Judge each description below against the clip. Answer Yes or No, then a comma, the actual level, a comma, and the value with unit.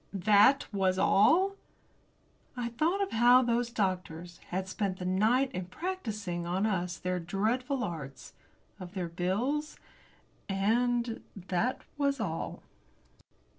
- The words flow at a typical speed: No, slow, 120 wpm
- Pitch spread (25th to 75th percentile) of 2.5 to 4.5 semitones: No, wide, 5.4 semitones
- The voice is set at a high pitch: Yes, high, 205 Hz